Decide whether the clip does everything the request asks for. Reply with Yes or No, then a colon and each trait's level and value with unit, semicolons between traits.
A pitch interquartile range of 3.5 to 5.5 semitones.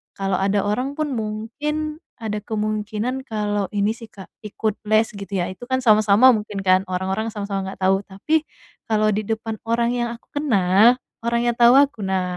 No: average, 2.7 semitones